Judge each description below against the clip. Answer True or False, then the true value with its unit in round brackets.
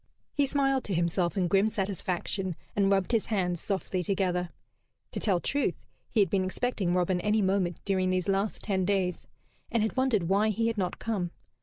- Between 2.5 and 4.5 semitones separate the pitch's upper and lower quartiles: True (2.9 semitones)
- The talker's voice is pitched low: False (195 Hz)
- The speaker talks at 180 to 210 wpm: True (185 wpm)